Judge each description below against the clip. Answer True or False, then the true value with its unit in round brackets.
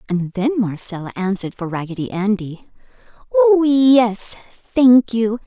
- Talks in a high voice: True (210 Hz)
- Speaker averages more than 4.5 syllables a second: False (4.3 syllables/s)